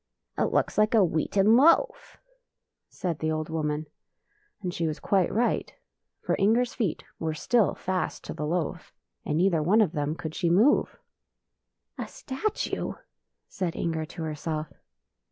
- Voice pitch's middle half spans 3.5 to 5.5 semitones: Yes, average, 5.2 semitones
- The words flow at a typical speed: Yes, average, 155 wpm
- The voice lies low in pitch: No, medium, 175 Hz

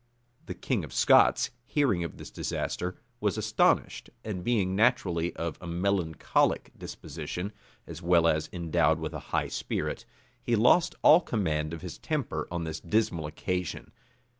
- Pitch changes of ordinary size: Yes, average, 4.2 semitones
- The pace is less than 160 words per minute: Yes, average, 150 wpm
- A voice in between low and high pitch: No, very low, 85 Hz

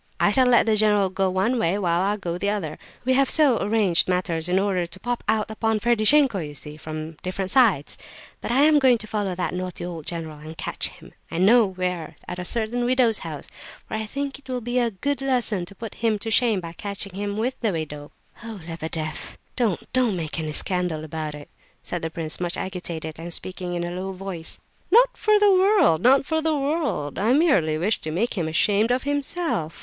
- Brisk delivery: Yes, fast, 215 wpm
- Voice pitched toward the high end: Yes, high, 195 Hz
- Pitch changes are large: Yes, wide, 6.2 semitones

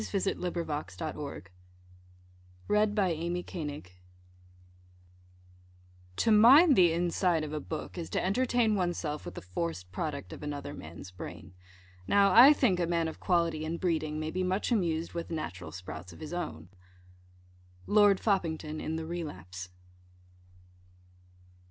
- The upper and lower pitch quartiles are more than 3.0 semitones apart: Yes, average, 4.2 semitones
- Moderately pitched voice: Yes, medium, 165 Hz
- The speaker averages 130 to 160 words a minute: Yes, average, 140 wpm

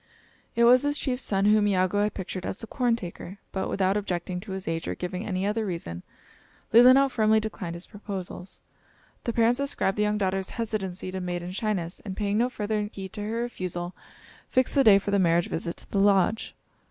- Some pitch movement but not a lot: Yes, average, 3.1 semitones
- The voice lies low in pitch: No, high, 200 Hz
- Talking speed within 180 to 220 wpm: Yes, average, 200 wpm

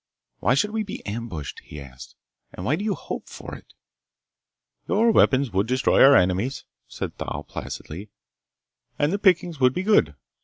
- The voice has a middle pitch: No, low, 130 Hz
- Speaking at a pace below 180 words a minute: Yes, average, 165 wpm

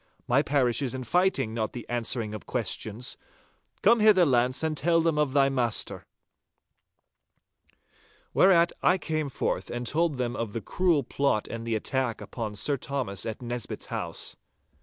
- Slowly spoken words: No, average, 155 wpm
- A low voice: Yes, low, 130 Hz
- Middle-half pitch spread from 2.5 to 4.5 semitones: No, average, 4.9 semitones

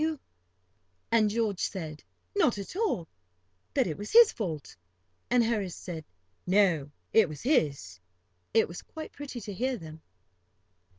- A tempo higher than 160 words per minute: No, average, 155 wpm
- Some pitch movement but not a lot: No, wide, 7.5 semitones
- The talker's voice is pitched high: Yes, high, 195 Hz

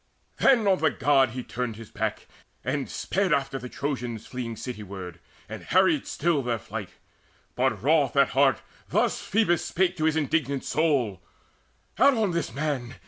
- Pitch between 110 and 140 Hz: Yes, low, 135 Hz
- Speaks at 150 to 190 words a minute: Yes, average, 160 wpm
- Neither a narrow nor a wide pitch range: Yes, average, 4.7 semitones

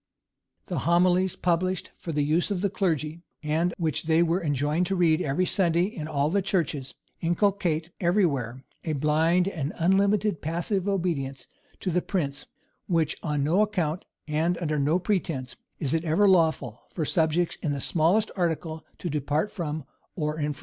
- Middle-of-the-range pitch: Yes, medium, 165 Hz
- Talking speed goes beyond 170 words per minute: No, average, 165 wpm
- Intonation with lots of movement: No, average, 3.2 semitones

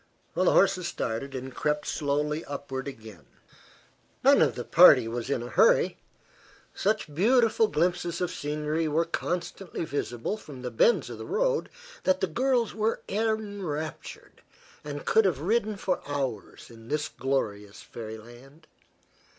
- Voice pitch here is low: No, medium, 150 Hz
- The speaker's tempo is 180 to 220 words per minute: No, average, 140 wpm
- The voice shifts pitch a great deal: Yes, wide, 6.4 semitones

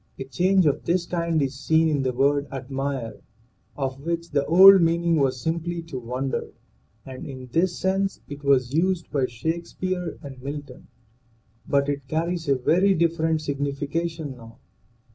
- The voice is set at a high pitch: No, medium, 150 Hz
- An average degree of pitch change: Yes, average, 3.8 semitones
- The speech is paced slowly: No, average, 160 wpm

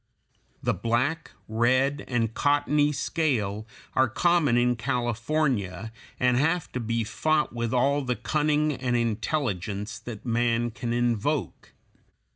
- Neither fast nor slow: No, slow, 120 wpm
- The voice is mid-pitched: No, low, 120 Hz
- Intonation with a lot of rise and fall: No, average, 4.1 semitones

